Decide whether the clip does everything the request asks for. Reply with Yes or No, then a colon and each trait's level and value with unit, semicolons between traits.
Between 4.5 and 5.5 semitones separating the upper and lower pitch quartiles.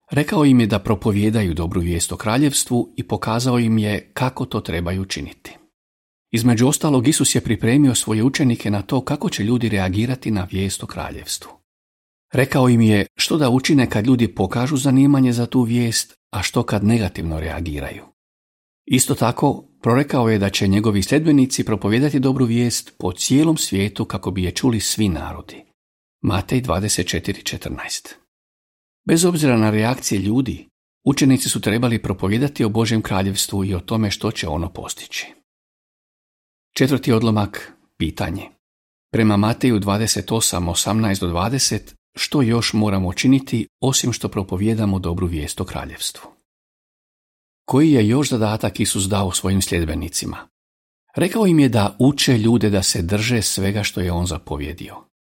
Yes: average, 4.9 semitones